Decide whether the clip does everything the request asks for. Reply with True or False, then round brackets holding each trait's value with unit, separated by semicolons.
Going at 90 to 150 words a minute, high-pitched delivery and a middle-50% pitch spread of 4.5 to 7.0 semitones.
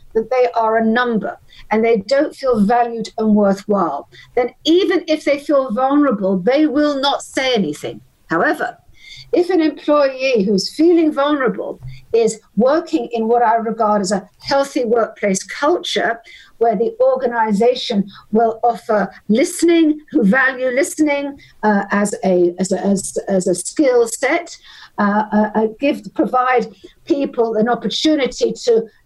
True (140 wpm; 240 Hz; 5.0 semitones)